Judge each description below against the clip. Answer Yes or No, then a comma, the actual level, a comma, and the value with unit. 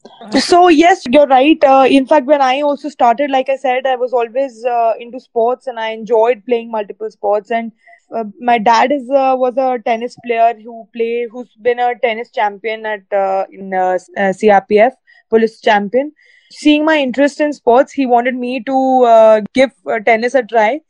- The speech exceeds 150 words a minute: Yes, average, 190 wpm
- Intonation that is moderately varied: Yes, average, 3.1 semitones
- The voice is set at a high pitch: Yes, high, 245 Hz